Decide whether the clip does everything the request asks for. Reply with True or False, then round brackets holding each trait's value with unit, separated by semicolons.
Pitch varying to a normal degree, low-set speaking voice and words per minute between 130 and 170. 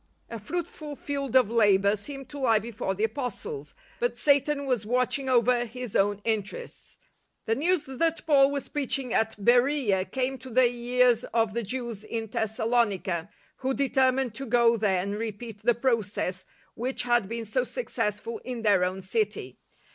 False (3.9 semitones; 235 Hz; 160 wpm)